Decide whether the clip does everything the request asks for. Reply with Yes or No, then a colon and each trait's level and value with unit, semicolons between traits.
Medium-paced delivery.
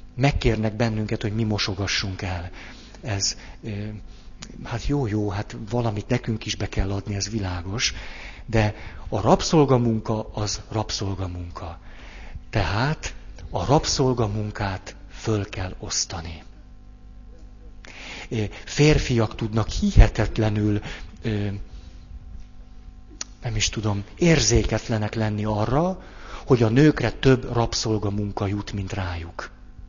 No: slow, 95 wpm